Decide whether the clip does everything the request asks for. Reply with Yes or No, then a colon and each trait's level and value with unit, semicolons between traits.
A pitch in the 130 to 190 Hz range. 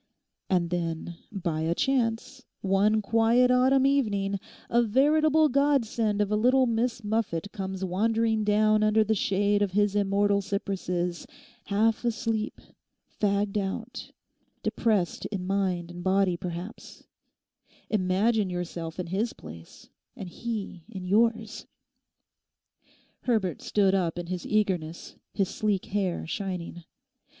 No: high, 205 Hz